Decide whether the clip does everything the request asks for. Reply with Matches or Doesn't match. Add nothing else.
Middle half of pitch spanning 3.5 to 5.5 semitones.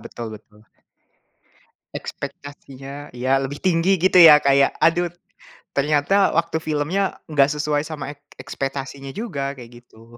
Doesn't match